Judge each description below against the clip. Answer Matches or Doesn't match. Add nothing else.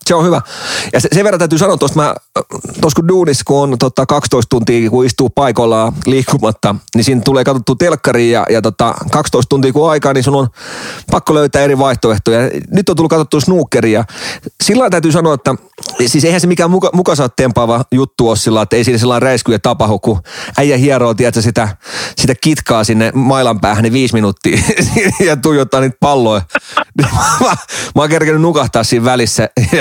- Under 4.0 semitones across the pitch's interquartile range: Doesn't match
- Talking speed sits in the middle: Doesn't match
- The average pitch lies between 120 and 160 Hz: Matches